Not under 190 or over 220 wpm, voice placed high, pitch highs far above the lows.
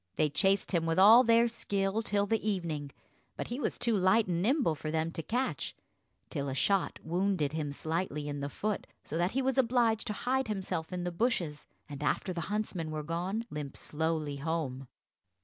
No: average, 195 wpm; medium, 180 Hz; wide, 5.7 semitones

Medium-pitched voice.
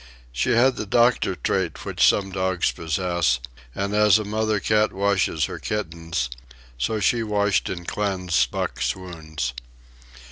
No: very low, 95 Hz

